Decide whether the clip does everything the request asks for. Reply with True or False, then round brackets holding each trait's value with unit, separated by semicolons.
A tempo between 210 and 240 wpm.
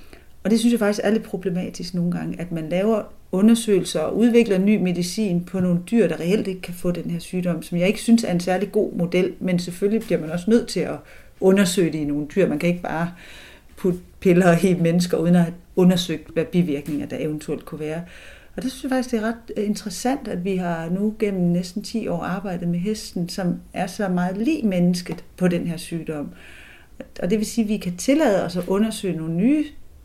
True (220 wpm)